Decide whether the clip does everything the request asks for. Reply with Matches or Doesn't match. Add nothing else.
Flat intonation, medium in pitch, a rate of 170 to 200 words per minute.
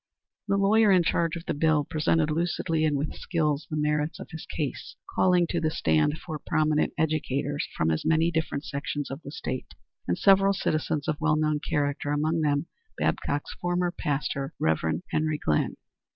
Matches